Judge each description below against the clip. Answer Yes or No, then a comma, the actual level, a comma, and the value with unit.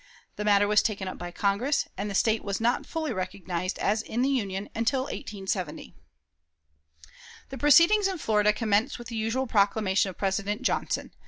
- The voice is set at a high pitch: Yes, high, 210 Hz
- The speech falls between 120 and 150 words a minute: No, average, 170 wpm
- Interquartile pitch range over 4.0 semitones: No, average, 3.6 semitones